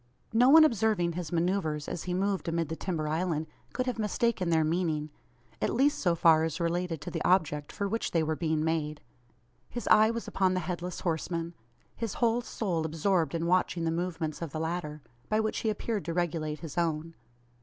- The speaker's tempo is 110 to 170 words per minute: No, average, 195 wpm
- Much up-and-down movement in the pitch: No, average, 3.6 semitones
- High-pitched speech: No, medium, 170 Hz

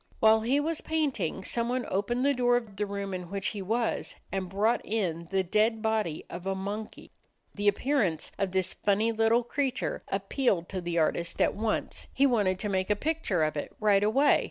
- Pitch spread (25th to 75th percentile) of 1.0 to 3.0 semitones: No, average, 4.0 semitones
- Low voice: No, high, 210 Hz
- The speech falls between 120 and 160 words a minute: No, average, 195 wpm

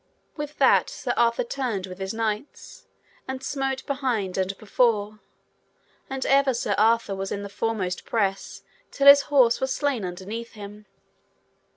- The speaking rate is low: No, average, 150 wpm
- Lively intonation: No, average, 4.8 semitones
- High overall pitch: Yes, high, 230 Hz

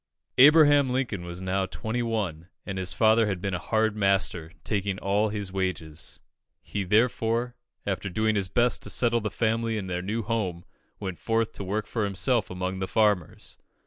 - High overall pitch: No, low, 105 Hz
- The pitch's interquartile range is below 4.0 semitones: Yes, average, 3.3 semitones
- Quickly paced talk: No, average, 175 wpm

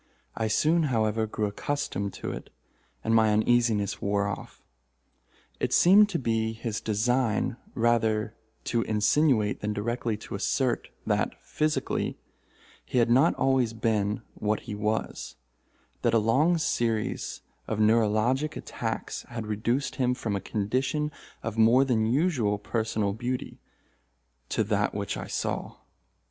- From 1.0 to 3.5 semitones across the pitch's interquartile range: Yes, average, 2.9 semitones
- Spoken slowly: Yes, slow, 130 wpm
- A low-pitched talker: Yes, low, 115 Hz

